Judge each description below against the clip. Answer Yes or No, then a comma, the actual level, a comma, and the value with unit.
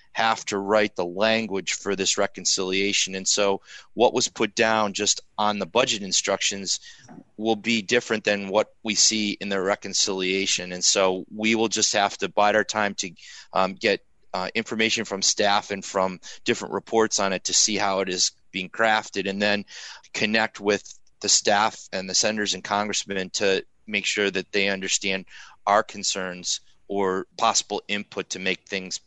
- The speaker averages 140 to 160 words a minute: No, average, 175 wpm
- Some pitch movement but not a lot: No, narrow, 2.0 semitones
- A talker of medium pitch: No, low, 100 Hz